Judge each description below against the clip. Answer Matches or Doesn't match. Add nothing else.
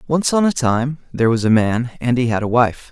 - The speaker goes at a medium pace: Doesn't match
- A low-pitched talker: Matches